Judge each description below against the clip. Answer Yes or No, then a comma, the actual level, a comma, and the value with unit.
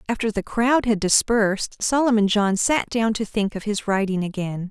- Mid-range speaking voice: No, high, 210 Hz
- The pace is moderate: Yes, average, 190 wpm